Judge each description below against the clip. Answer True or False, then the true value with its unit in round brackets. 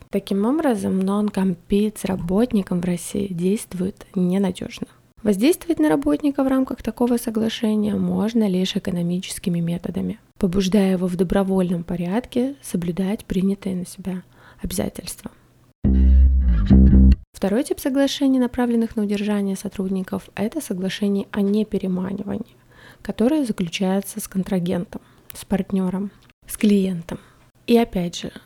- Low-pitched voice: False (200 Hz)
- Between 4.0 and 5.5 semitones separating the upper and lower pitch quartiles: False (3.3 semitones)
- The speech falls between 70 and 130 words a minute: True (110 wpm)